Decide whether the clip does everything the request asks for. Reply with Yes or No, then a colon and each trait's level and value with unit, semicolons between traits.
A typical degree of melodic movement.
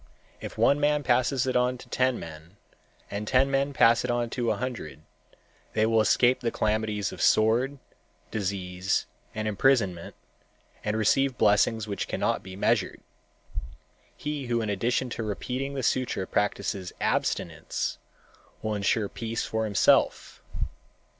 Yes: average, 3.8 semitones